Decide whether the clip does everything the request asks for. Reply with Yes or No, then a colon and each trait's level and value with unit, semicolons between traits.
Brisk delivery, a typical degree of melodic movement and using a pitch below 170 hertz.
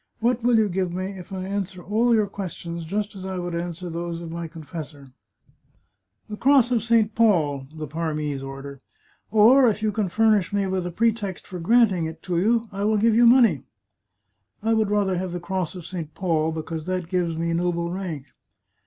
No: fast, 215 wpm; average, 4.3 semitones; medium, 185 Hz